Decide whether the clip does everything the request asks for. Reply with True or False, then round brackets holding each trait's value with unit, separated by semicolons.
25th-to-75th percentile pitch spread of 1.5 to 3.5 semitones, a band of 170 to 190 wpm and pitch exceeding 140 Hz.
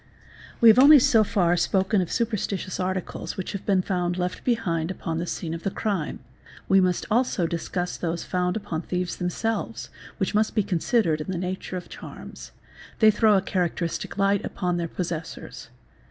True (3.0 semitones; 175 wpm; 185 Hz)